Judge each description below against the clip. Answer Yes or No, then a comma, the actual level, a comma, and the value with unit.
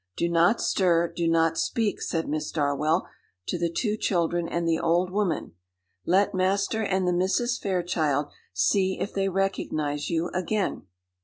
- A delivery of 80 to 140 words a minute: No, average, 155 wpm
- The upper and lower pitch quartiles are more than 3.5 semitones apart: No, average, 2.9 semitones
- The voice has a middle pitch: Yes, medium, 175 Hz